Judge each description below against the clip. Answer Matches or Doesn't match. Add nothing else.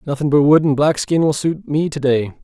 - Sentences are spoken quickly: Matches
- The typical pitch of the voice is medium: Matches